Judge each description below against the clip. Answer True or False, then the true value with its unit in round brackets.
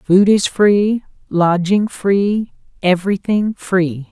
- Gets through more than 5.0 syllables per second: False (3.1 syllables/s)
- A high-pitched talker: True (195 Hz)